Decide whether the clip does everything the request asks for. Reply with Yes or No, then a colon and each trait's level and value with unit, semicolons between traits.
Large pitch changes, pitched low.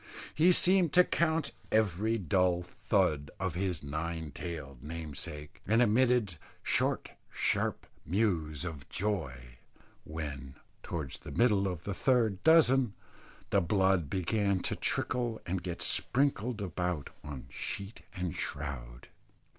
Yes: wide, 6.2 semitones; very low, 90 Hz